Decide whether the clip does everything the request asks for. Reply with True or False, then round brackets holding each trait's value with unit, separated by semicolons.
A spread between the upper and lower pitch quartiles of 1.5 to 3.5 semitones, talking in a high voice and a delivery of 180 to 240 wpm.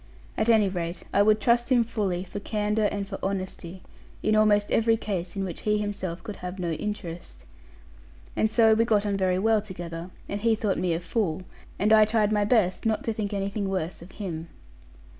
True (2.8 semitones; 205 Hz; 200 wpm)